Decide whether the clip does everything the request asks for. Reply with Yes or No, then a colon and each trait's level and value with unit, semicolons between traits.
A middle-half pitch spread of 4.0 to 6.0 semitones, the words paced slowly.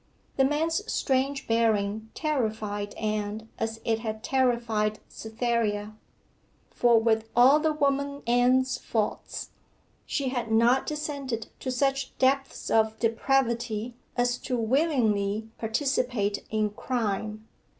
No: average, 3.5 semitones; slow, 110 wpm